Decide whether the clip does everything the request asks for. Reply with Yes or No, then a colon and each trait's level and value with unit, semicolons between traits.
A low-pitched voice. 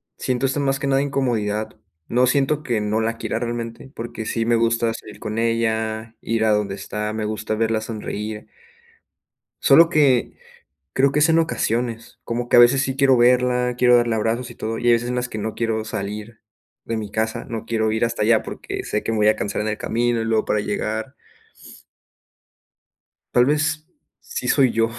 Yes: low, 115 Hz